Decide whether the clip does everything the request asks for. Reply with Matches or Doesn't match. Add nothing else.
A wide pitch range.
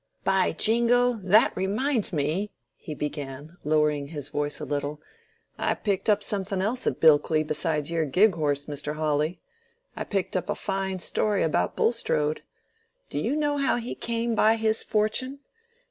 Matches